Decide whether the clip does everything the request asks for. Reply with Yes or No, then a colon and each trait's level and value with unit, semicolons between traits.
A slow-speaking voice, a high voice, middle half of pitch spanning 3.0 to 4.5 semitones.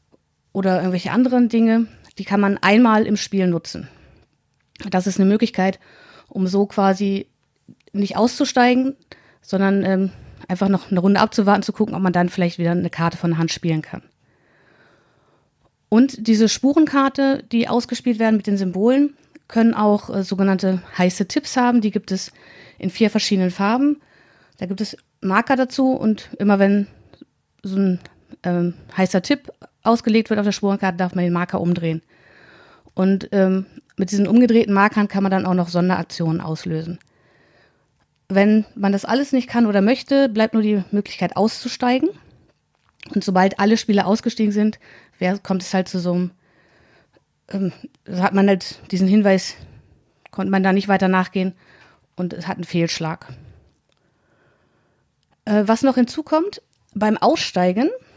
No: average, 155 wpm; high, 200 Hz; average, 3.5 semitones